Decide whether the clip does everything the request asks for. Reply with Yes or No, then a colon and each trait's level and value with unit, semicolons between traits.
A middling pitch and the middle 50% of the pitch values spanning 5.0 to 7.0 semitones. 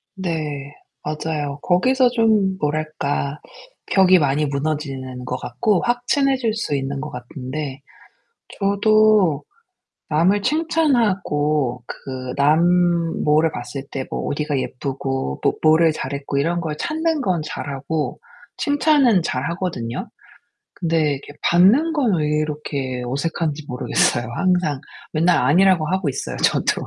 Yes: medium, 155 Hz; average, 5.3 semitones